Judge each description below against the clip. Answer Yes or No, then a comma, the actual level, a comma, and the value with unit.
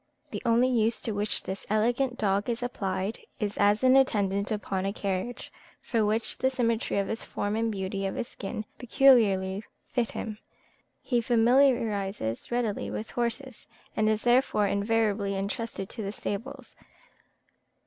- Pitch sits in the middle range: No, high, 215 Hz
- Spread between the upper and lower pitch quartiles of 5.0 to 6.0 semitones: No, average, 3.3 semitones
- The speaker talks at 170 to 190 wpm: No, average, 150 wpm